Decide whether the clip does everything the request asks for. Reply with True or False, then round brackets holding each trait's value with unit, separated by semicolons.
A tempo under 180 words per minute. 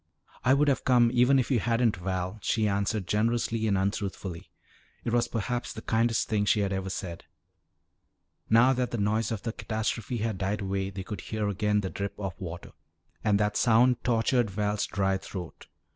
False (185 wpm)